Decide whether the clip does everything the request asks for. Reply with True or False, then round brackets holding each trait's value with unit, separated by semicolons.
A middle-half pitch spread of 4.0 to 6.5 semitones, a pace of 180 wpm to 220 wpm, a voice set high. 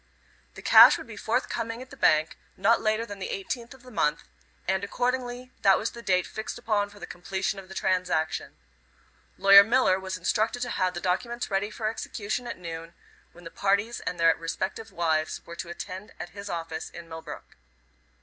True (4.4 semitones; 190 wpm; 195 Hz)